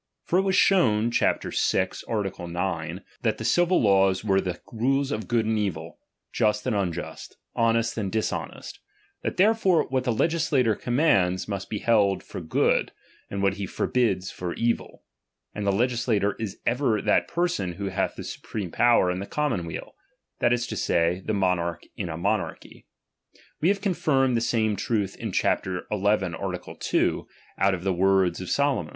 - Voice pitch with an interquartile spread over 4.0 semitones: Yes, average, 4.4 semitones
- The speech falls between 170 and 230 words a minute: Yes, average, 180 wpm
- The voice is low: Yes, low, 105 Hz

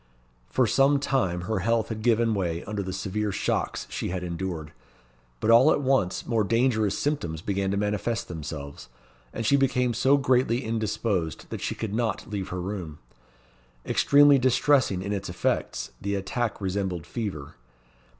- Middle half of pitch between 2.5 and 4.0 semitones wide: No, average, 4.5 semitones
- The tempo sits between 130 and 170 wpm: Yes, average, 160 wpm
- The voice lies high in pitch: No, low, 105 Hz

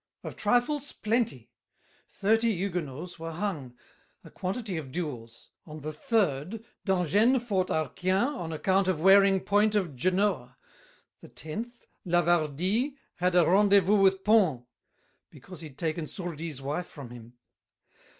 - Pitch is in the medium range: Yes, medium, 180 Hz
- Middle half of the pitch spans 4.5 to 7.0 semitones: Yes, average, 4.9 semitones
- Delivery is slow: Yes, slow, 125 wpm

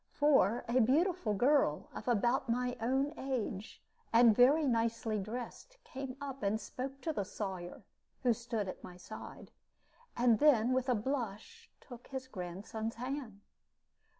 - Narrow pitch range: No, average, 3.8 semitones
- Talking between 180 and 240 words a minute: No, average, 145 wpm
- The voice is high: Yes, high, 240 Hz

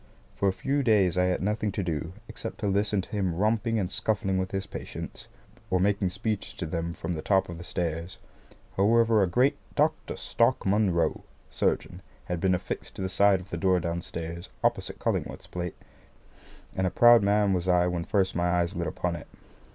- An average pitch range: Yes, average, 3.0 semitones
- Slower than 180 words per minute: No, average, 195 wpm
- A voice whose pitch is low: Yes, very low, 95 Hz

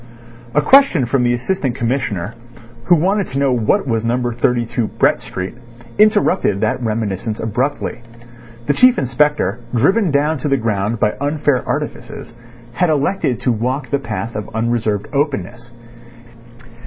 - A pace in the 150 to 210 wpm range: No, average, 140 wpm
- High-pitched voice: No, low, 125 Hz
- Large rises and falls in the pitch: No, average, 4.3 semitones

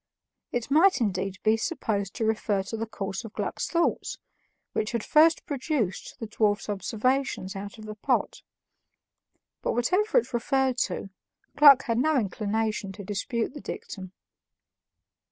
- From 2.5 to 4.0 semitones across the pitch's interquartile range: No, average, 4.8 semitones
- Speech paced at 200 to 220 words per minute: No, average, 145 wpm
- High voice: Yes, high, 225 Hz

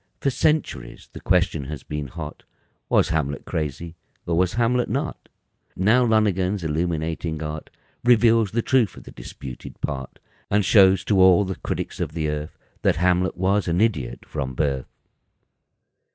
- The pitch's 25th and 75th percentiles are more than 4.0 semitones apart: Yes, wide, 5.6 semitones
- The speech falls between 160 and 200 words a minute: No, average, 150 wpm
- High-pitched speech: No, very low, 90 Hz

